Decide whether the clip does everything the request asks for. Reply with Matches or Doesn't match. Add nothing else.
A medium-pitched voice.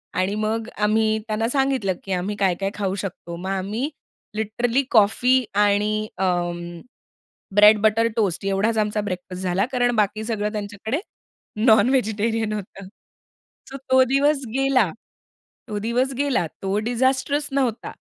Doesn't match